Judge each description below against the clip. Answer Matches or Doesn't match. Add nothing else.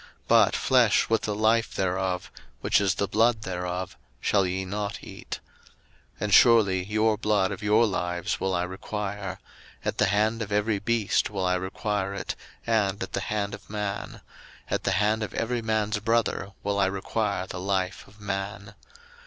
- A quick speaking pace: Doesn't match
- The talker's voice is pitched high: Doesn't match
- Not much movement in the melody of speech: Matches